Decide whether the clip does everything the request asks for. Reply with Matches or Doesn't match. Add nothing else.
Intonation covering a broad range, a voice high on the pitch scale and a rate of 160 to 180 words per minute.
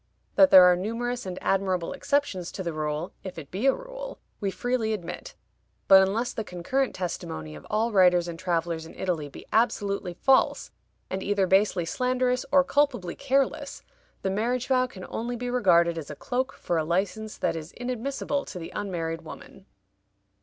Matches